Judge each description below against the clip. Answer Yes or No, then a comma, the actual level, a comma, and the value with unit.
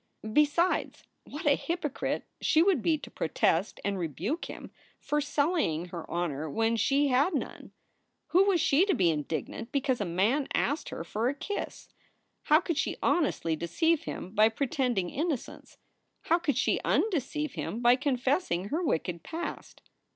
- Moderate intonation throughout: No, wide, 8.5 semitones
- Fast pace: No, average, 160 wpm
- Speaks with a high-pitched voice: Yes, very high, 275 Hz